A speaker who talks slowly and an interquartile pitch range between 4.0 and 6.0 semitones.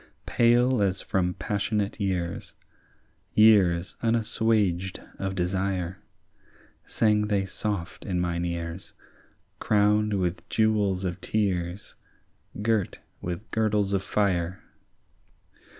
No: slow, 95 wpm; average, 2.9 semitones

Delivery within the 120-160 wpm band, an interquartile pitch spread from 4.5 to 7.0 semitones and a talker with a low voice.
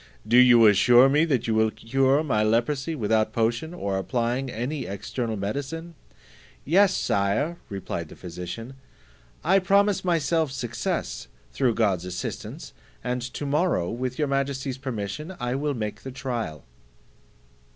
Yes: average, 140 wpm; average, 4.9 semitones; low, 125 Hz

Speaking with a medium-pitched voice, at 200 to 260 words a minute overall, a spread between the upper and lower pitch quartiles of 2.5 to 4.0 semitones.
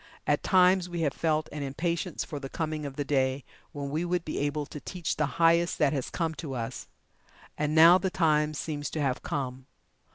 Yes: medium, 150 Hz; fast, 205 wpm; average, 2.9 semitones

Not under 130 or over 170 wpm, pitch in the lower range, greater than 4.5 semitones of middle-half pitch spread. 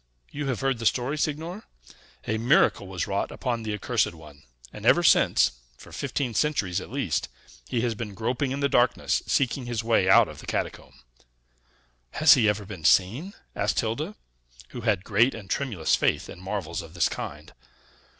No: average, 180 wpm; low, 115 Hz; wide, 5.5 semitones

